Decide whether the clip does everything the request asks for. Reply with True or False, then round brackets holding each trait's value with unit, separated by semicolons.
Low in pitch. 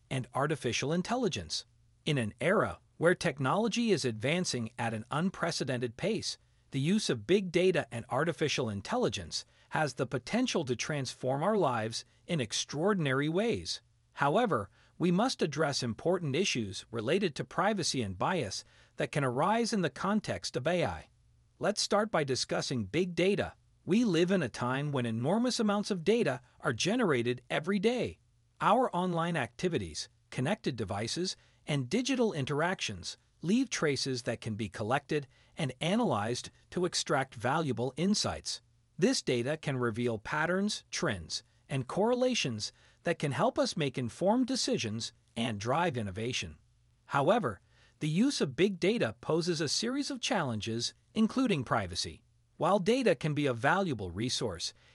False (150 Hz)